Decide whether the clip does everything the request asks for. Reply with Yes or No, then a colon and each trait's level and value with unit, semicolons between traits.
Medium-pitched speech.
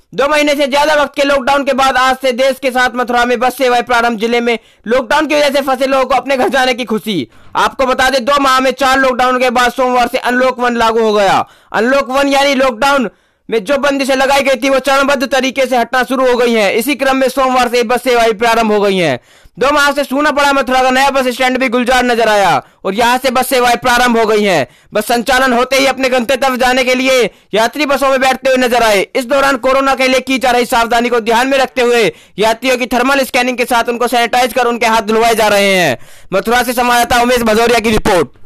No: very high, 255 Hz